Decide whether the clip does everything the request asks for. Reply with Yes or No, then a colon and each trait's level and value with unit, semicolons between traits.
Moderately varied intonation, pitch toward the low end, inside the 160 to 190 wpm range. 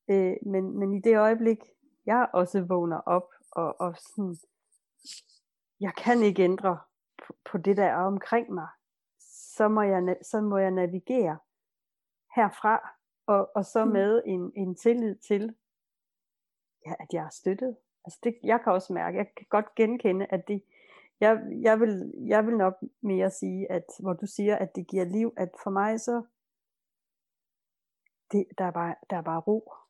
No: average, 3.1 semitones; high, 200 Hz; average, 165 wpm